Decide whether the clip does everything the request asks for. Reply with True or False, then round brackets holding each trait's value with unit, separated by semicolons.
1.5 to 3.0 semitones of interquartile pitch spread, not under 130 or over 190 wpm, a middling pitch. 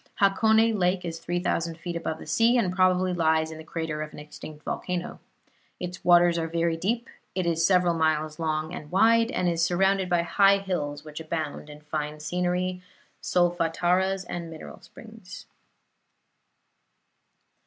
True (2.5 semitones; 155 wpm; 175 Hz)